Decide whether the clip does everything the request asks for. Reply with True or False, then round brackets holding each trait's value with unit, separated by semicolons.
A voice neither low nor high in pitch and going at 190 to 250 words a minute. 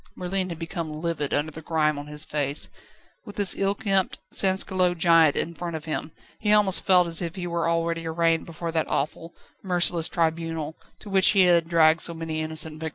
True (165 Hz; 200 wpm)